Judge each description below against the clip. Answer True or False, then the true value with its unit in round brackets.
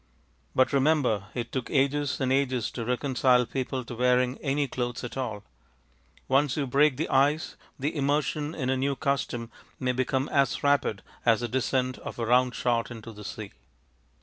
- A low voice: True (130 Hz)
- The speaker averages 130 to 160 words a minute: False (175 wpm)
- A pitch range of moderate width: False (2.3 semitones)